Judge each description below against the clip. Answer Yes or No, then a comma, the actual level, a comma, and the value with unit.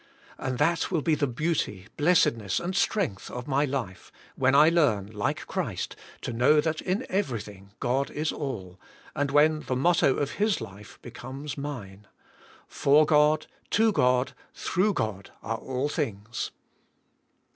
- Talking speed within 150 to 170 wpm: Yes, average, 155 wpm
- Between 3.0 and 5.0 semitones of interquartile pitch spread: No, wide, 5.4 semitones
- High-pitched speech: No, medium, 140 Hz